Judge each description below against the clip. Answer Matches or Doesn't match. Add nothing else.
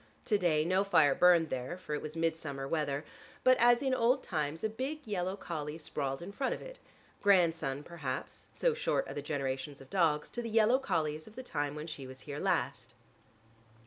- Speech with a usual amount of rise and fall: Doesn't match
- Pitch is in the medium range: Matches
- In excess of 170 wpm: Matches